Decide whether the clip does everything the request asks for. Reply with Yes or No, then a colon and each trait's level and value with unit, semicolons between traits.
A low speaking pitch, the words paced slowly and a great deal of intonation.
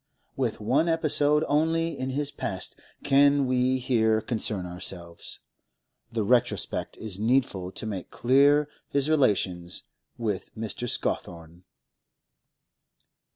Yes: low, 120 Hz; slow, 110 wpm; wide, 6.2 semitones